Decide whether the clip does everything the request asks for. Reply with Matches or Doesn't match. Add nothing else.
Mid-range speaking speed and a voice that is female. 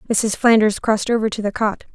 Doesn't match